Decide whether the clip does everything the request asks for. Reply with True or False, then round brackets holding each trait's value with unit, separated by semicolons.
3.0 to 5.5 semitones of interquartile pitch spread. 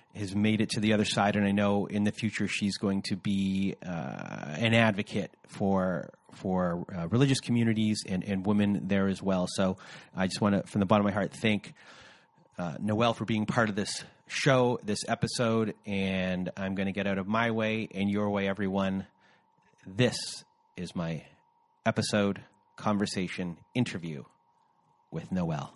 False (2.5 semitones)